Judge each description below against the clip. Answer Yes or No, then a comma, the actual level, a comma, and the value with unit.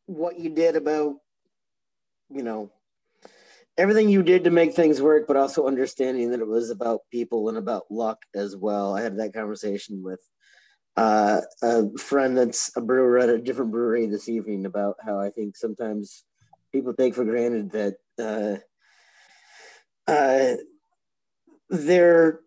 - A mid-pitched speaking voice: No, low, 120 Hz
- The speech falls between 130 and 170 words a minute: Yes, average, 150 wpm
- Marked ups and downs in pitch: Yes, wide, 6.6 semitones